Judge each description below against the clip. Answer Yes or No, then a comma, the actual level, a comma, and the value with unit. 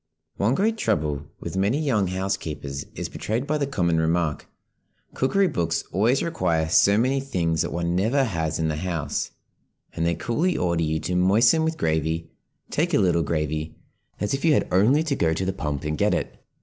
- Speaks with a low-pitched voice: Yes, very low, 90 Hz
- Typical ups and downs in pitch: No, wide, 8.6 semitones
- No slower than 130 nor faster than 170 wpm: No, average, 190 wpm